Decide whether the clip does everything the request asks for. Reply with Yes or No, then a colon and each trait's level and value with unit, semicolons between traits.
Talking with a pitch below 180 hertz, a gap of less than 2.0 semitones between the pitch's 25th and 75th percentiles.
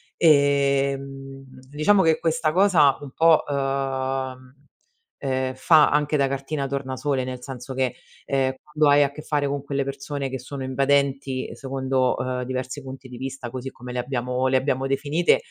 Yes: low, 135 Hz; narrow, 1.5 semitones